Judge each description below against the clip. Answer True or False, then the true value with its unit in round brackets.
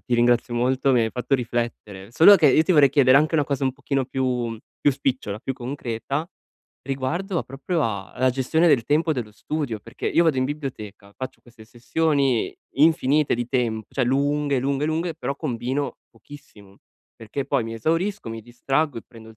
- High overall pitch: False (130 Hz)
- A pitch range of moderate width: True (3.6 semitones)